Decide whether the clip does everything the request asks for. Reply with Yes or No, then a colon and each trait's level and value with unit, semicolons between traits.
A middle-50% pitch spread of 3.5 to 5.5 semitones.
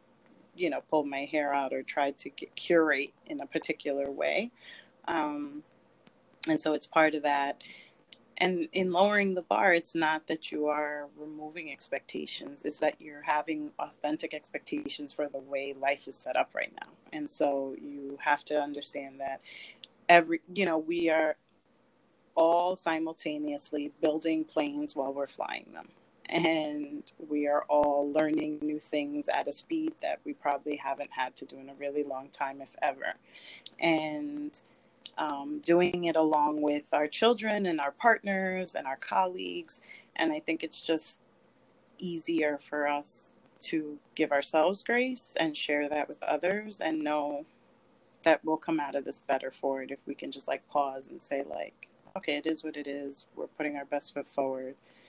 No: average, 2.8 semitones